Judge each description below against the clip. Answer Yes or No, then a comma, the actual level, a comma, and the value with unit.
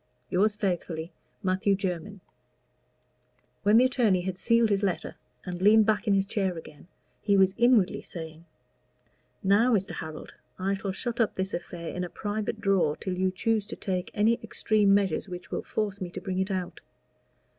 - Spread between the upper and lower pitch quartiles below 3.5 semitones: Yes, narrow, 2.6 semitones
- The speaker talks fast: No, average, 175 wpm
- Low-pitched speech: No, high, 195 Hz